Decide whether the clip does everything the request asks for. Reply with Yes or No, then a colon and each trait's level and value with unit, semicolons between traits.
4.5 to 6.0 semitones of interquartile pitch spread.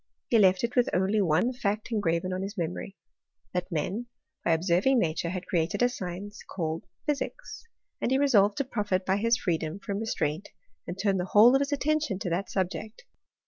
Yes: average, 4.8 semitones